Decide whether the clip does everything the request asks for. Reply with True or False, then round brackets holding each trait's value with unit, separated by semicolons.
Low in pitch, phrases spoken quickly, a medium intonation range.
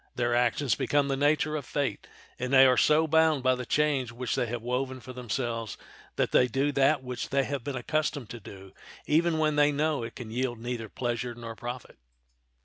True (130 Hz; 210 wpm; 3.3 semitones)